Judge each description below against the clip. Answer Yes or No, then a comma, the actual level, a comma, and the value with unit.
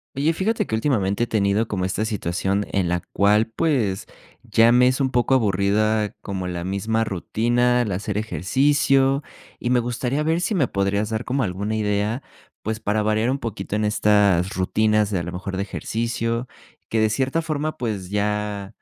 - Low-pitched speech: Yes, low, 110 Hz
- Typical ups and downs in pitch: Yes, average, 3.7 semitones